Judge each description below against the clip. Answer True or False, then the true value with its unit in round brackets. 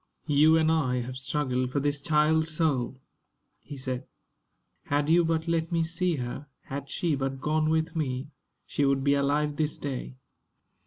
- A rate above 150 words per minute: True (165 wpm)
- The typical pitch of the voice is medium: True (145 Hz)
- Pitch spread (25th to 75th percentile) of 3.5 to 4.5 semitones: False (3.0 semitones)